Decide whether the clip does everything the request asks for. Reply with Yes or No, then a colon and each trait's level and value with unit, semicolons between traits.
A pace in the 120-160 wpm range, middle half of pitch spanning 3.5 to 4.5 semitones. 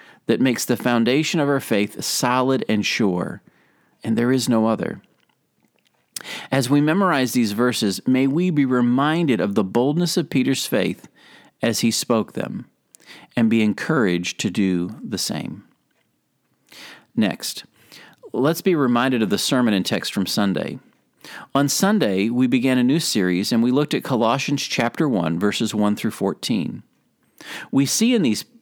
Yes: average, 155 wpm; average, 4.0 semitones